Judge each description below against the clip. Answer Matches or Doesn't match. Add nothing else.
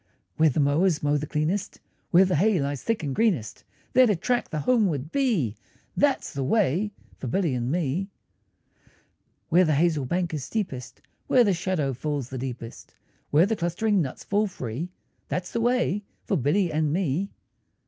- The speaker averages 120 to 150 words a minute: Doesn't match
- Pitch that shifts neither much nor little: Doesn't match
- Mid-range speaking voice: Matches